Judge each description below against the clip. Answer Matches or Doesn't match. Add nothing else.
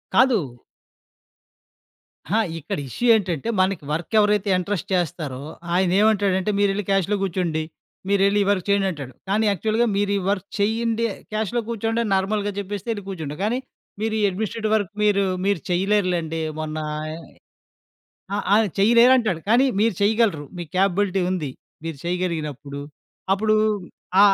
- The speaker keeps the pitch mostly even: Doesn't match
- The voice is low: Doesn't match